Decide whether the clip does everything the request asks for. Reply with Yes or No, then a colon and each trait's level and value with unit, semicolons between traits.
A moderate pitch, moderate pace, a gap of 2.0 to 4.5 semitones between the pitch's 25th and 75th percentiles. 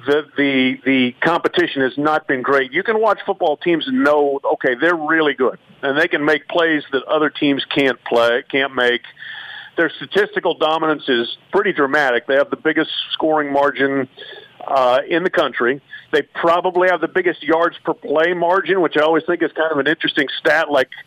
Yes: medium, 155 Hz; average, 190 wpm; average, 3.6 semitones